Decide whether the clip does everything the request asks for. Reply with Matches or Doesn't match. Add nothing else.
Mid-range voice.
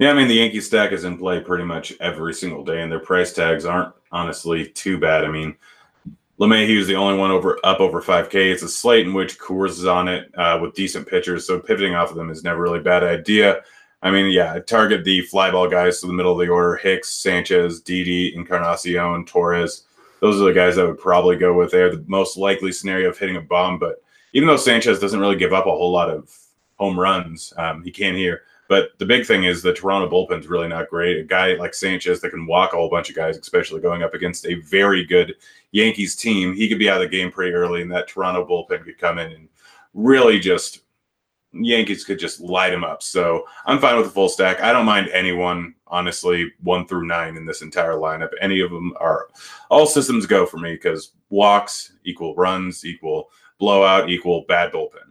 Doesn't match